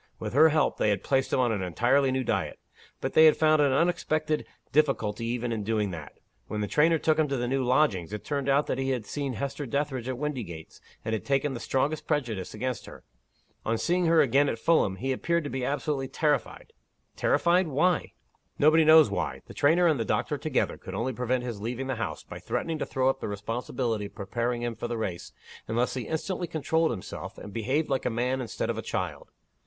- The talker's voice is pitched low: Yes, low, 130 Hz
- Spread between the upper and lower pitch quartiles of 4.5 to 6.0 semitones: Yes, average, 4.8 semitones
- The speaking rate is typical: No, fast, 220 wpm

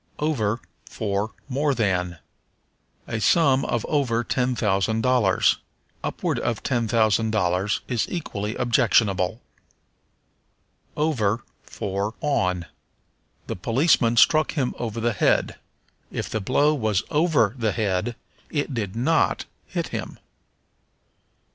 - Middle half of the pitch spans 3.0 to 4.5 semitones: Yes, average, 4.2 semitones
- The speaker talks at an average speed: No, slow, 115 wpm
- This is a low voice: Yes, low, 115 Hz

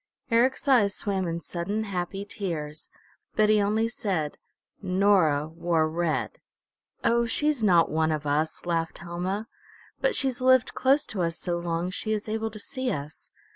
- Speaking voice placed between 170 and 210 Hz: Yes, high, 190 Hz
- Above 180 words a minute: No, average, 160 wpm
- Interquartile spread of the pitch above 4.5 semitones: Yes, average, 4.9 semitones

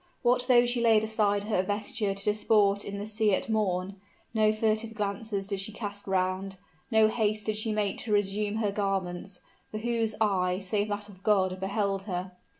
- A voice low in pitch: No, high, 205 Hz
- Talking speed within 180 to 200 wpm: Yes, average, 185 wpm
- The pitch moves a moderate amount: No, narrow, 1.8 semitones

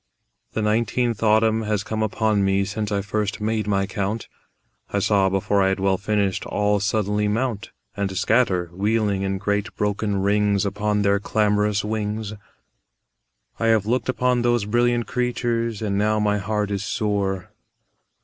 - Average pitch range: No, narrow, 1.7 semitones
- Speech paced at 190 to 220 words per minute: No, average, 155 wpm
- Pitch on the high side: No, low, 105 Hz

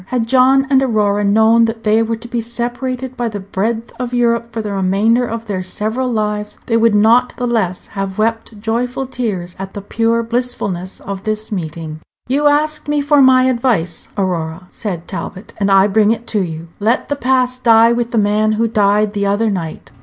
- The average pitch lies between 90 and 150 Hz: No, high, 225 Hz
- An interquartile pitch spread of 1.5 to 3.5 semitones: Yes, average, 3.2 semitones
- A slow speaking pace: No, average, 200 wpm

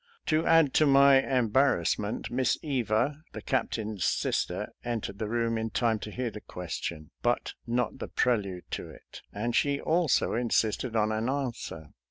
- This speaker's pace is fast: No, average, 170 wpm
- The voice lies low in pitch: Yes, low, 120 Hz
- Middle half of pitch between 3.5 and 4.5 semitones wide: Yes, average, 3.9 semitones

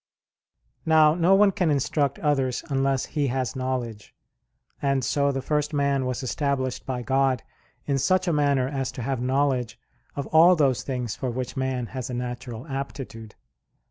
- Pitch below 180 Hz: Yes, low, 135 Hz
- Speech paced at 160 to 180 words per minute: Yes, average, 165 wpm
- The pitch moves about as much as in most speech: No, narrow, 2.2 semitones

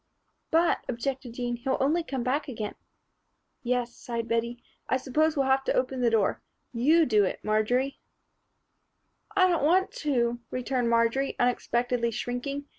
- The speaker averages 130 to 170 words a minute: Yes, average, 150 wpm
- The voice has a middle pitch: No, very high, 250 Hz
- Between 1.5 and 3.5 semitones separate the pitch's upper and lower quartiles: Yes, average, 2.8 semitones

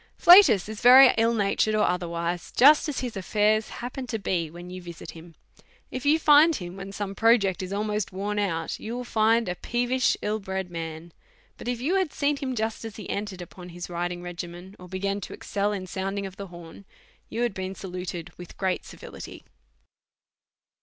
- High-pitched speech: Yes, high, 200 Hz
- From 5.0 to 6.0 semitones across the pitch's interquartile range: No, average, 4.5 semitones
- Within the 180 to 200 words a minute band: Yes, average, 195 wpm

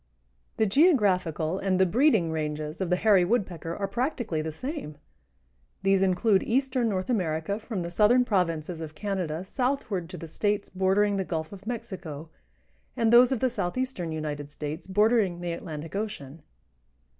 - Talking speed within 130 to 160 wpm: Yes, average, 155 wpm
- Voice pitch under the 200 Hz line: Yes, high, 190 Hz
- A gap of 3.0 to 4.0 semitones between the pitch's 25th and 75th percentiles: No, average, 5.2 semitones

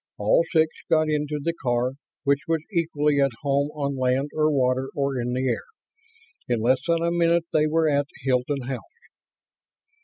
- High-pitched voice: No, medium, 145 Hz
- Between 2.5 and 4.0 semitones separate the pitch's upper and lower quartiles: Yes, average, 3.2 semitones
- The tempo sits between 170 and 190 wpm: Yes, average, 175 wpm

